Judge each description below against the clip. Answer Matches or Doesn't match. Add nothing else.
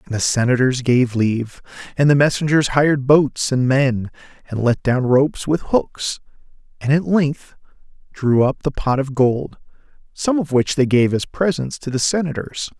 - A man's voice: Matches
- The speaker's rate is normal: Matches